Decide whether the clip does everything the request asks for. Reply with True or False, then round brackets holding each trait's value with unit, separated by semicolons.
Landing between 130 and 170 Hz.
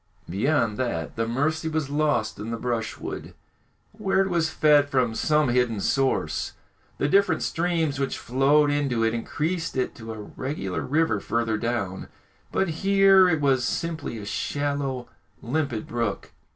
True (135 Hz)